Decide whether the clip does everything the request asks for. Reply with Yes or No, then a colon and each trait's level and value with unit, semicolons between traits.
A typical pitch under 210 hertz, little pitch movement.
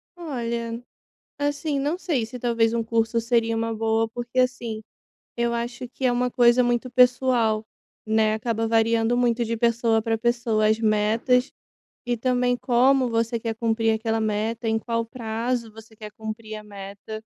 No: high, 230 Hz; narrow, 1.6 semitones